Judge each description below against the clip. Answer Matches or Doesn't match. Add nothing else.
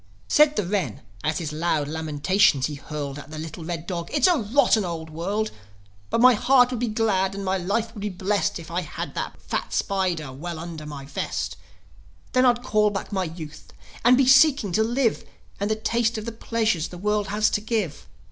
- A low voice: Doesn't match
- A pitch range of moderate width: Doesn't match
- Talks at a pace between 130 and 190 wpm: Doesn't match